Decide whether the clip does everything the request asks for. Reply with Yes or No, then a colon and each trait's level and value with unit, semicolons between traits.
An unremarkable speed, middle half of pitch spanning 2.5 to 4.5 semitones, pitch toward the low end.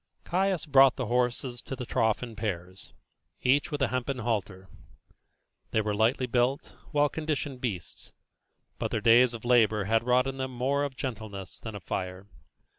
Yes: average, 170 wpm; average, 3.6 semitones; low, 120 Hz